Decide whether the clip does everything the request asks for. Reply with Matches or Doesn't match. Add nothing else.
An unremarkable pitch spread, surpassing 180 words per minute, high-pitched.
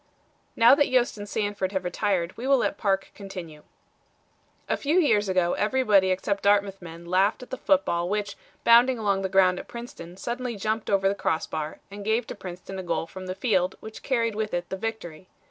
Matches